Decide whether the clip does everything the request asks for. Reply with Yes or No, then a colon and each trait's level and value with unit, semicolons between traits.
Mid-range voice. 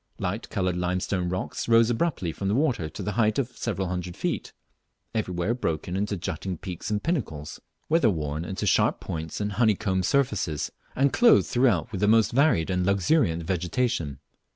No: low, 100 Hz